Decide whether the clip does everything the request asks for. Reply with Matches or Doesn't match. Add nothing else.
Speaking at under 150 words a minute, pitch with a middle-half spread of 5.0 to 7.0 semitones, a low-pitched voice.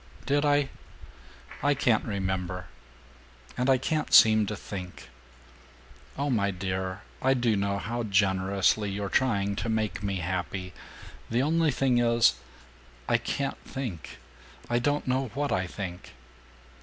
Matches